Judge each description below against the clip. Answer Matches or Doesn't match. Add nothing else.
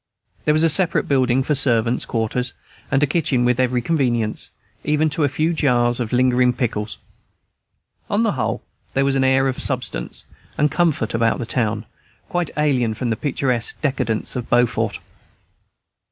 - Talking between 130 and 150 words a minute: Doesn't match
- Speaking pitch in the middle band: Doesn't match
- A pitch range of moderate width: Matches